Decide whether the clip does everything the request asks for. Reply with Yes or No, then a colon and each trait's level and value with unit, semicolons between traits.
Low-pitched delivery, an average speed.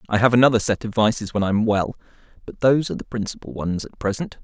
No: low, 110 Hz; fast, 230 wpm